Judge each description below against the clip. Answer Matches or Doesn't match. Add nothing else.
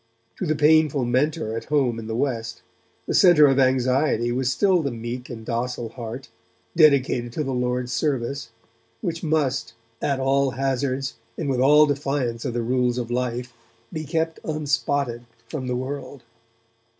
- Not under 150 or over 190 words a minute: Matches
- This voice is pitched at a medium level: Doesn't match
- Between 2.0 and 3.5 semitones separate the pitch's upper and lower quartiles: Matches